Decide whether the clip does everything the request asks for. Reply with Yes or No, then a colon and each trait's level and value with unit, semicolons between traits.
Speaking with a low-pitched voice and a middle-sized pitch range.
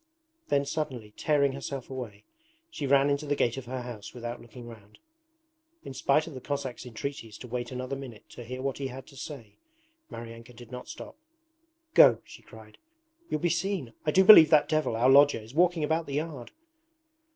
Yes: low, 130 Hz; average, 3.5 semitones